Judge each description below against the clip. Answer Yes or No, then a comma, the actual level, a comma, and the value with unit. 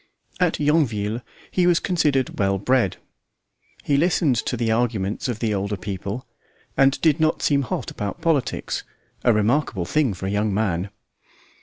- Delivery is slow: No, average, 155 wpm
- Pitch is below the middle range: Yes, low, 120 Hz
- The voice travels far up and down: Yes, wide, 6.3 semitones